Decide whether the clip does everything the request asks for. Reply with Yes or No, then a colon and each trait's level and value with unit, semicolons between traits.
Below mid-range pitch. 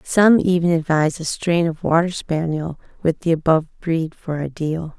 No: medium, 165 Hz